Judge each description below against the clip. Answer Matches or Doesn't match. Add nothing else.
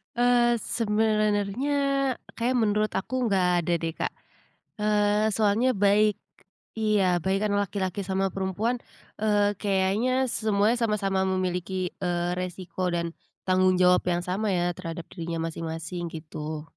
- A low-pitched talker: Doesn't match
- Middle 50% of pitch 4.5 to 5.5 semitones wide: Doesn't match